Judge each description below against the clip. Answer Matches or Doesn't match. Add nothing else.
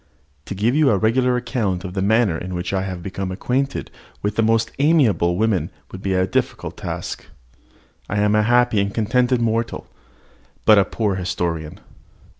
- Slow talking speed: Doesn't match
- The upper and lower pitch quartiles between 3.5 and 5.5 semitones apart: Matches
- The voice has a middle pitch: Doesn't match